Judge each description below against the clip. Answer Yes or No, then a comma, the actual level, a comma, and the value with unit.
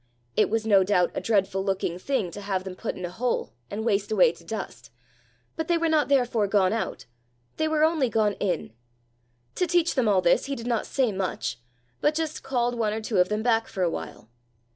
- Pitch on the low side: No, high, 220 Hz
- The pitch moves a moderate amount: No, wide, 5.7 semitones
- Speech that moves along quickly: Yes, fast, 220 wpm